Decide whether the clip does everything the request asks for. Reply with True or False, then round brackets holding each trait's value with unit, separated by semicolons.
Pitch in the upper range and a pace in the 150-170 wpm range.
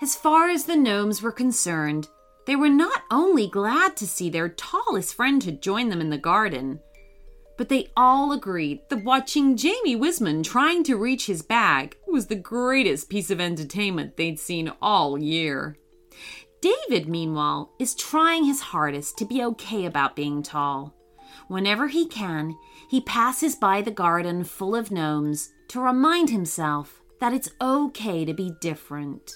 True (200 Hz; 160 wpm)